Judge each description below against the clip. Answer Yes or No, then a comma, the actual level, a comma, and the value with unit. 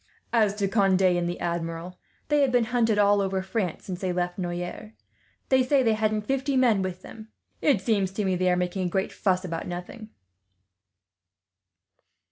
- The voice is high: Yes, high, 195 Hz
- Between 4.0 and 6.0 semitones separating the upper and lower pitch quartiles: No, average, 3.6 semitones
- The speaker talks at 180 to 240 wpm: Yes, average, 185 wpm